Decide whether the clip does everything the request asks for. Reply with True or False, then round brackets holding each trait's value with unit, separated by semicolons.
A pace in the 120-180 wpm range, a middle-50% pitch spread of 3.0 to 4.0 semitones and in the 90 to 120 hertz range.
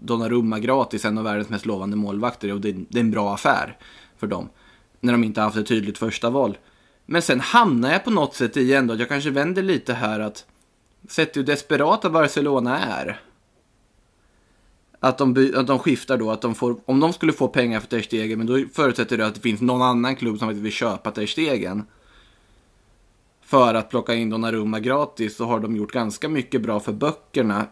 False (195 wpm; 3.3 semitones; 115 Hz)